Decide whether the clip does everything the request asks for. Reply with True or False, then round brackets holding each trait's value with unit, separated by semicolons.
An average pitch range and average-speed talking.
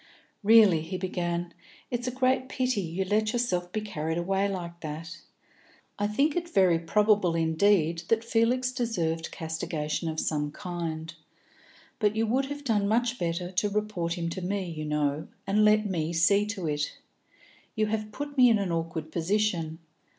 True (4.6 semitones; 165 wpm)